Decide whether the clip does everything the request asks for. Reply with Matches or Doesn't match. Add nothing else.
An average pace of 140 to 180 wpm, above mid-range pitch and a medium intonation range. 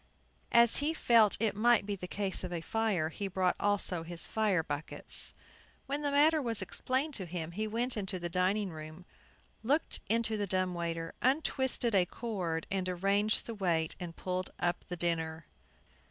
Matches